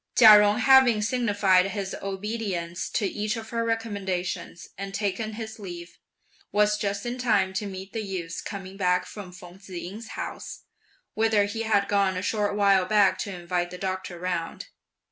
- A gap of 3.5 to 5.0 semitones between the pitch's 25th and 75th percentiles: No, narrow, 2.6 semitones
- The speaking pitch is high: Yes, high, 200 Hz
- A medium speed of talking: Yes, average, 170 wpm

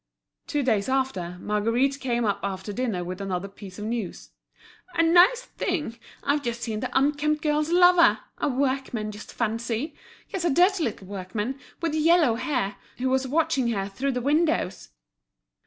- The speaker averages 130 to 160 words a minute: Yes, average, 155 wpm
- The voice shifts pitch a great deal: Yes, wide, 6.2 semitones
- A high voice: Yes, very high, 255 Hz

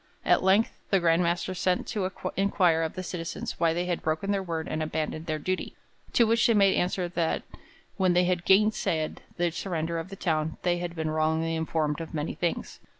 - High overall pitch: No, medium, 175 Hz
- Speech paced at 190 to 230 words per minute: Yes, fast, 205 wpm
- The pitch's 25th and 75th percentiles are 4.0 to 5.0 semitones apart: No, narrow, 2.6 semitones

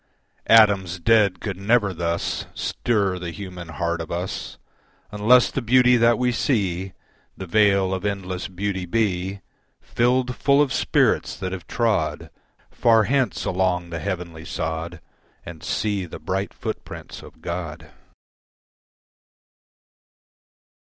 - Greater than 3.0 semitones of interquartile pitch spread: Yes, average, 4.3 semitones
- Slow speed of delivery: Yes, slow, 125 wpm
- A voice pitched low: Yes, very low, 95 Hz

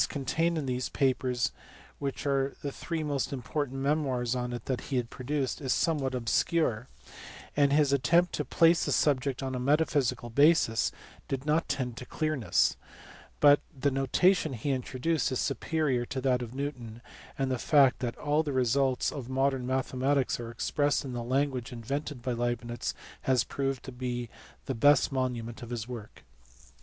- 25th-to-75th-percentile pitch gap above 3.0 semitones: No, average, 2.7 semitones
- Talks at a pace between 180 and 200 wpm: No, average, 165 wpm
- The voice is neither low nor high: No, low, 130 Hz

